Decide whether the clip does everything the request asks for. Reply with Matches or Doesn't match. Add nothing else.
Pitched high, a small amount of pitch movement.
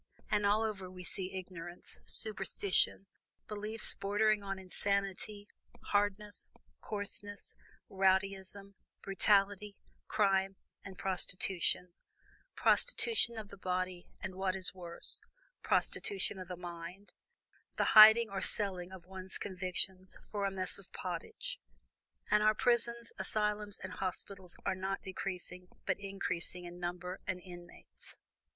Matches